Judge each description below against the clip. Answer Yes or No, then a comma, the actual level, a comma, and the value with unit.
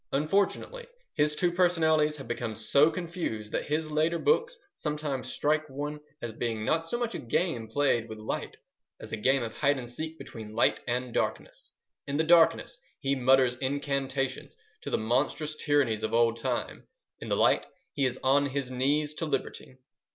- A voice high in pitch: No, medium, 140 Hz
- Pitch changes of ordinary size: Yes, average, 4.3 semitones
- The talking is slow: No, average, 175 wpm